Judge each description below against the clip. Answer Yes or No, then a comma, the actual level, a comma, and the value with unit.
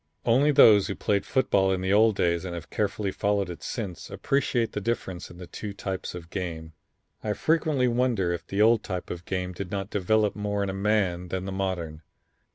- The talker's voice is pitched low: Yes, low, 100 Hz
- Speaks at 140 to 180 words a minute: No, fast, 205 wpm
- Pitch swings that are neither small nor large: Yes, average, 3.0 semitones